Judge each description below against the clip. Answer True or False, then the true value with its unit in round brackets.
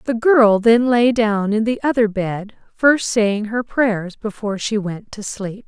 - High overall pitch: True (220 Hz)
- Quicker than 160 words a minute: True (190 wpm)